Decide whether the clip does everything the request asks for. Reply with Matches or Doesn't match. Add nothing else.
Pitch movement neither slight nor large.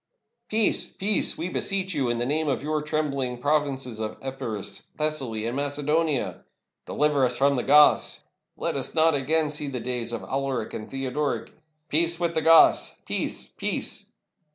Matches